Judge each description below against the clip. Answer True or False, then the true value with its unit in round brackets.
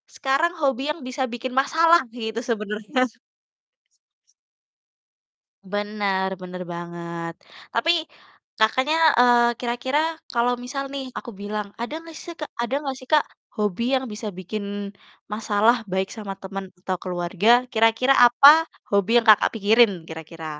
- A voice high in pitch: True (225 Hz)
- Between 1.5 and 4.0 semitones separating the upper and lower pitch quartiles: False (4.6 semitones)